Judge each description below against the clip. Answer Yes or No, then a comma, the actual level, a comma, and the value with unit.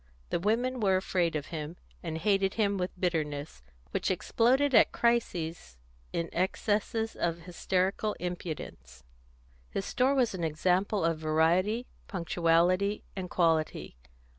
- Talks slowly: Yes, slow, 125 wpm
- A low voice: No, medium, 180 Hz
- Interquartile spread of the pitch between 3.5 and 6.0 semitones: Yes, average, 4.1 semitones